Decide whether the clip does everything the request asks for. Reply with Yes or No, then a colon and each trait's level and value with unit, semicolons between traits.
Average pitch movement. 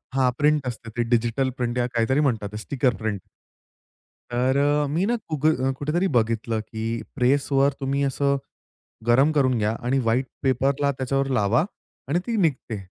Yes: average, 3.2 semitones